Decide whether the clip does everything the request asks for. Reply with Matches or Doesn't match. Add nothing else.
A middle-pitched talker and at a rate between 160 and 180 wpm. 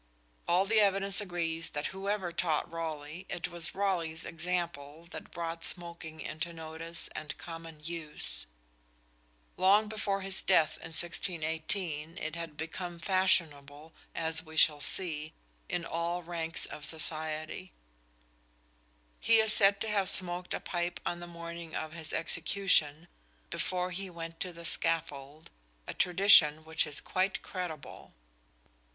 Doesn't match